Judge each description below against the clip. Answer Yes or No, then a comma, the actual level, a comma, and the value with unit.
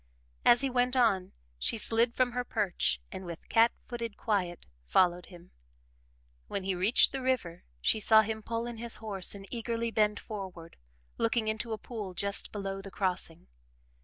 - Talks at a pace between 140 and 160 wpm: No, average, 170 wpm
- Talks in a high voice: Yes, high, 215 Hz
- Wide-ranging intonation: No, average, 3.7 semitones